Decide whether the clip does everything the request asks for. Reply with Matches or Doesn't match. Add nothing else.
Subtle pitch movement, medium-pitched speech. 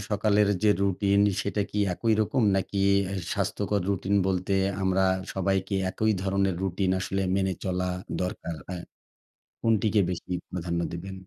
Doesn't match